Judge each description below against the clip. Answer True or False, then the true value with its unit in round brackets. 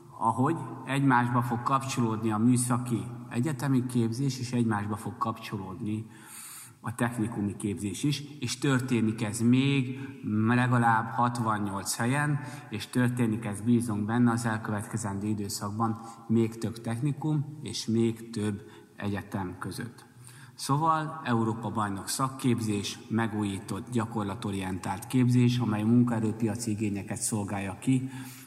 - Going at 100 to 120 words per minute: True (110 wpm)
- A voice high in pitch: False (115 Hz)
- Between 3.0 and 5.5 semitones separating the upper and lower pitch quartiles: False (2.6 semitones)